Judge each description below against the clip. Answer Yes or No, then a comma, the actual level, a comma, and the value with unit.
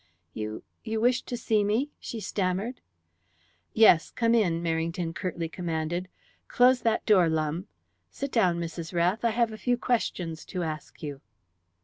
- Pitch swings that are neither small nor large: No, wide, 5.7 semitones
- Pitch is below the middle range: No, medium, 185 Hz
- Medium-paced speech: Yes, average, 150 wpm